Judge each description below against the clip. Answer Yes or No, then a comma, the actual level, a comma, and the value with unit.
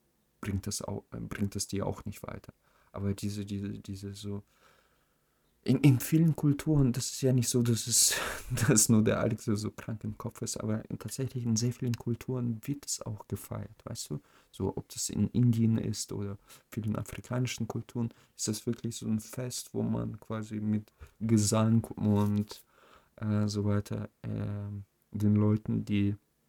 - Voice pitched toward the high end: No, low, 110 Hz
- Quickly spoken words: No, average, 170 wpm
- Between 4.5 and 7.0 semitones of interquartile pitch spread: No, narrow, 2.6 semitones